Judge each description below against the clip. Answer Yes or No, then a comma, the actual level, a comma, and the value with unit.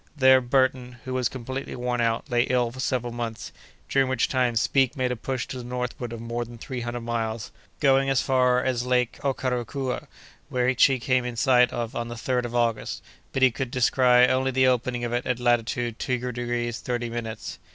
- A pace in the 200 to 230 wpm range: Yes, fast, 205 wpm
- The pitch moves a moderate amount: No, narrow, 1.4 semitones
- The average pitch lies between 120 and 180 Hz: Yes, low, 125 Hz